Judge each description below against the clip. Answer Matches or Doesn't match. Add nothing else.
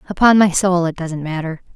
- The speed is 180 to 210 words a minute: Matches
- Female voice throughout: Matches